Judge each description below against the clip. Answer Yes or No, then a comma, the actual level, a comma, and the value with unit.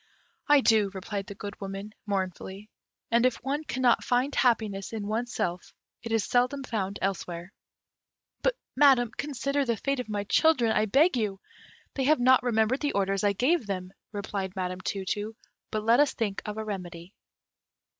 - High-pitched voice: Yes, high, 220 Hz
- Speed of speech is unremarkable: Yes, average, 175 wpm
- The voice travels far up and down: No, average, 4.4 semitones